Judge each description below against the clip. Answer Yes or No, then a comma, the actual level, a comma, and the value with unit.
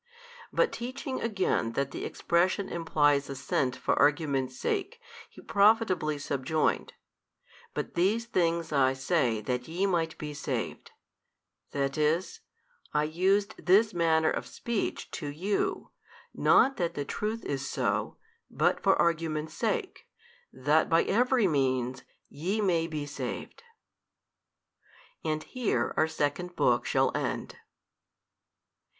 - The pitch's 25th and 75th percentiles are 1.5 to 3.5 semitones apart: No, average, 5.3 semitones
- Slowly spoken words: Yes, slow, 120 wpm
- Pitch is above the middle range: No, medium, 160 Hz